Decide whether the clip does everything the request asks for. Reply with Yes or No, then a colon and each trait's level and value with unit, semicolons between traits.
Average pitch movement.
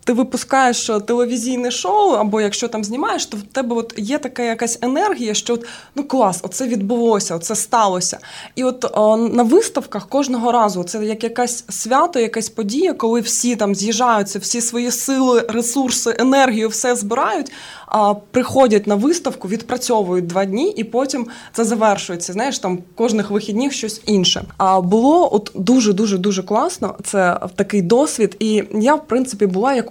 Yes: average, 3.1 semitones